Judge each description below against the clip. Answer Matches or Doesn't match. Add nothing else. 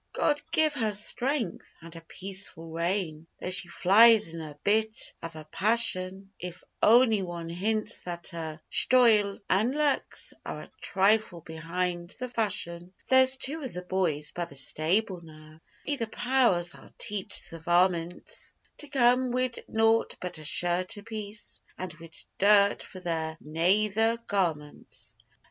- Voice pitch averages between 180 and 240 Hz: Matches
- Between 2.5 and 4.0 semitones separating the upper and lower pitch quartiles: Doesn't match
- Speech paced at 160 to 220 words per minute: Doesn't match